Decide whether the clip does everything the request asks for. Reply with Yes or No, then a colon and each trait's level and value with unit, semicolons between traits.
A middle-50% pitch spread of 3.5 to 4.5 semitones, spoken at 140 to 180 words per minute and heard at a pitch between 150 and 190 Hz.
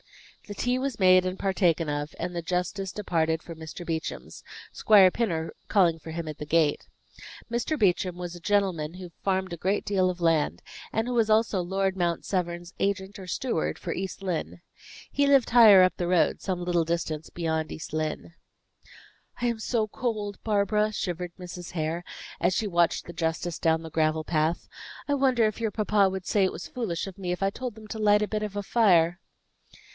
No: average, 3.8 semitones; average, 195 wpm; medium, 185 Hz